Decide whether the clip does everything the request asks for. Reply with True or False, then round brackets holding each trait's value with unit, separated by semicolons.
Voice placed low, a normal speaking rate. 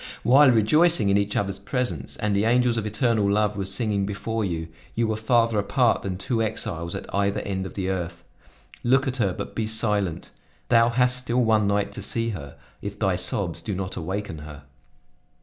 True (105 Hz; 195 wpm)